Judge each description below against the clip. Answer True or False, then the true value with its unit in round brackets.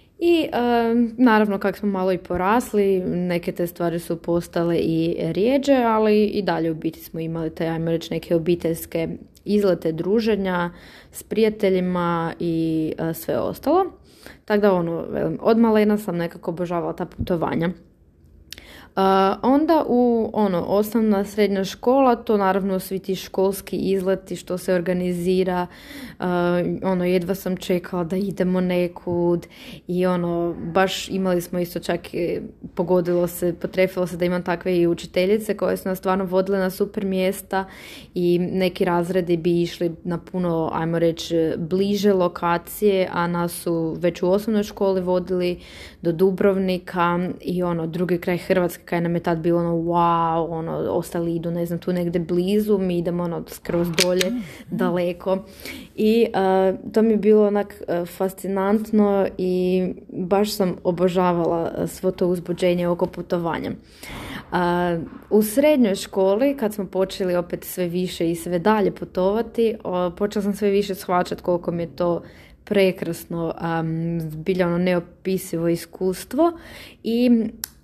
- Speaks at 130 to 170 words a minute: True (145 wpm)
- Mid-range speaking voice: True (180 Hz)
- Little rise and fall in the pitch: True (2.3 semitones)